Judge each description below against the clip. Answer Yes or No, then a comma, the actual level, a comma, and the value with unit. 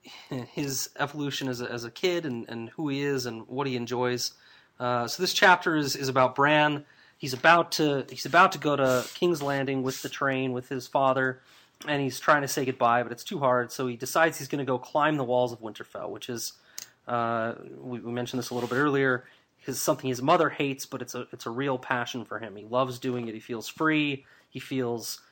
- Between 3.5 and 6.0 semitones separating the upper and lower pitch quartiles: No, average, 2.7 semitones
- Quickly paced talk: Yes, fast, 225 wpm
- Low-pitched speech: Yes, low, 130 Hz